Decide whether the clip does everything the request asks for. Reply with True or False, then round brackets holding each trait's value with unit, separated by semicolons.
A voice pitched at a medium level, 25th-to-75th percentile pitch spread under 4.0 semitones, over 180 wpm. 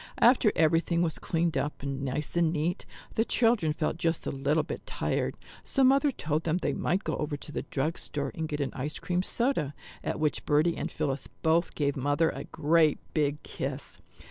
True (155 Hz; 2.8 semitones; 195 wpm)